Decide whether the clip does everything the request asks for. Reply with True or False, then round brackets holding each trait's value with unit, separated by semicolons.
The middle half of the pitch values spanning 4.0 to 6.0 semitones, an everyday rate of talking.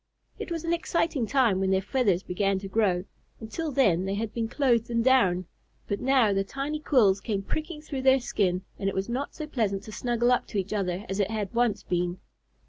False (5.3 semitones; 220 wpm)